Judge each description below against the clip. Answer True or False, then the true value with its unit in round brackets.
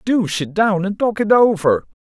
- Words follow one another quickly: True (210 wpm)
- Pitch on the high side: True (195 Hz)